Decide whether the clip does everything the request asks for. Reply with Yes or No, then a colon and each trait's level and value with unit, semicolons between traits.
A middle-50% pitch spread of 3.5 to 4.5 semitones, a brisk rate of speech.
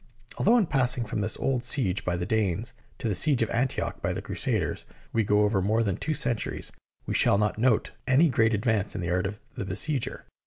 Yes: average, 4.0 semitones; fast, 220 wpm